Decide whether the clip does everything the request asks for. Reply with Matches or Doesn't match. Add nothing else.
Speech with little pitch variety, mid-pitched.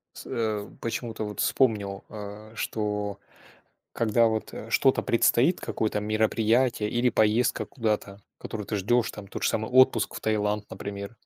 Doesn't match